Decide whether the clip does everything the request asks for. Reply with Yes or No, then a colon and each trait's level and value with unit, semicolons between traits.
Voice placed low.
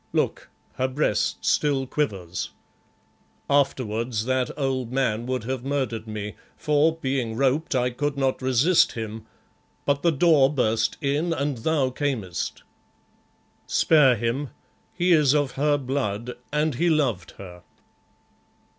Yes: low, 130 Hz